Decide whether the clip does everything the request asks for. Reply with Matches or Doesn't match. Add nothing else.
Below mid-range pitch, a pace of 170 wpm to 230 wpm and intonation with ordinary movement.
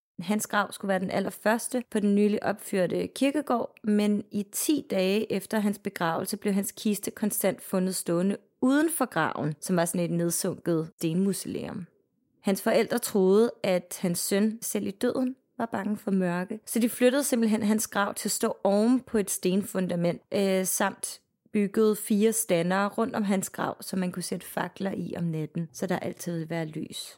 Doesn't match